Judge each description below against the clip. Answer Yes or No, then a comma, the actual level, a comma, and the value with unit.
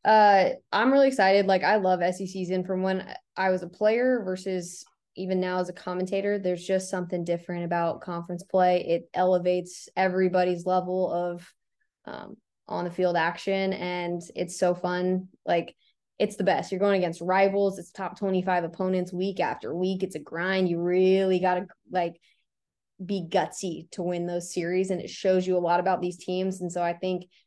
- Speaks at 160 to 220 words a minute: Yes, average, 180 wpm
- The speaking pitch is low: No, medium, 185 Hz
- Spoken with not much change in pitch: Yes, narrow, 1.1 semitones